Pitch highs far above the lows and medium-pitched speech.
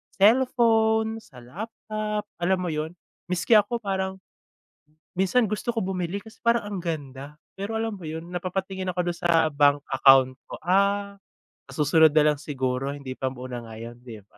Yes: wide, 6.3 semitones; medium, 180 Hz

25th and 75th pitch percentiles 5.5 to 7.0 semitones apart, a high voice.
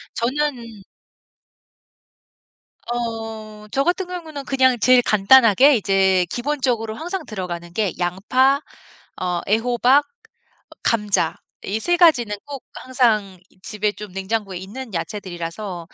No: average, 5.1 semitones; high, 225 Hz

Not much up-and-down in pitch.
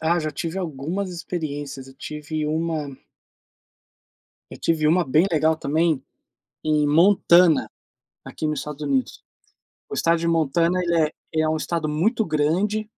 Yes: narrow, 2.2 semitones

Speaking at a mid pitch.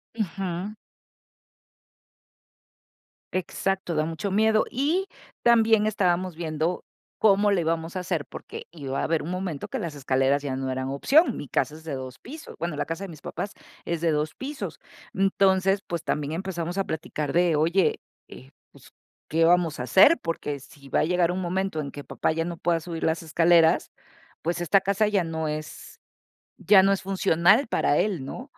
Yes: medium, 170 Hz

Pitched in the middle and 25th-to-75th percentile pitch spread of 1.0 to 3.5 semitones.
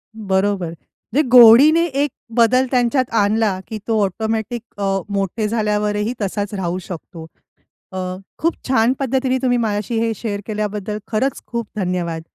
No: high, 220 Hz; average, 3.1 semitones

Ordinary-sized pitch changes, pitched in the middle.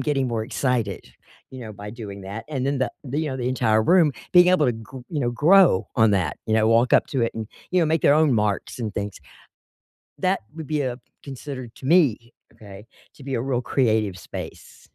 No: average, 4.5 semitones; low, 125 Hz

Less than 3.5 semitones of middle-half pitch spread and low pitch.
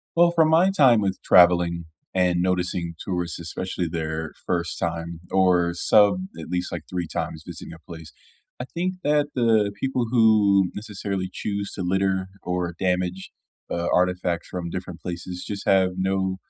Yes: average, 2.7 semitones; very low, 90 Hz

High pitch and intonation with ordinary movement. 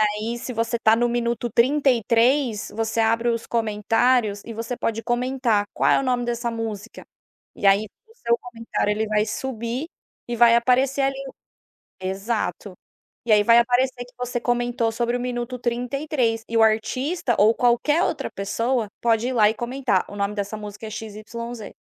No: high, 235 Hz; narrow, 2.0 semitones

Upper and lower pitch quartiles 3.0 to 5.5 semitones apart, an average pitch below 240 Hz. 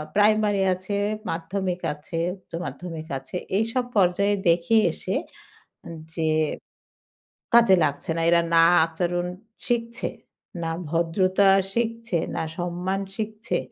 Yes: average, 3.9 semitones; medium, 185 Hz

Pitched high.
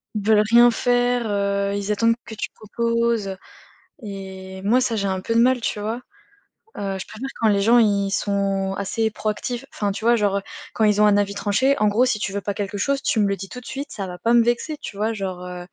Yes: high, 210 Hz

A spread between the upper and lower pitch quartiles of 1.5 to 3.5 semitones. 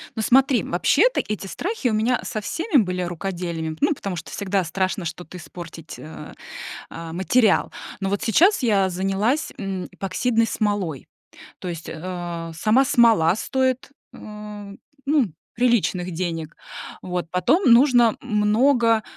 No: average, 5.3 semitones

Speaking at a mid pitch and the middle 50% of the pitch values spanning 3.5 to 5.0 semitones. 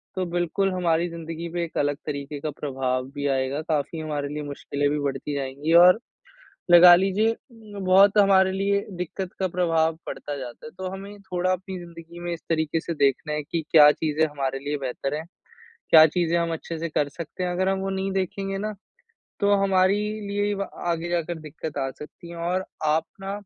Yes: medium, 170 Hz; average, 4.0 semitones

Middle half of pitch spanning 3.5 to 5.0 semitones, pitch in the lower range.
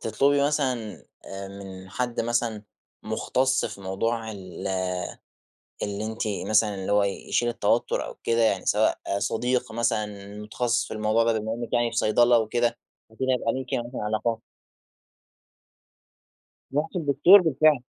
No: average, 2.8 semitones; low, 115 Hz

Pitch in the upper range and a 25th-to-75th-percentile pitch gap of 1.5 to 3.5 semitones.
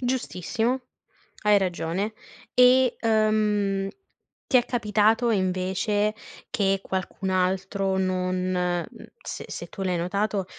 Yes: high, 200 Hz; average, 2.7 semitones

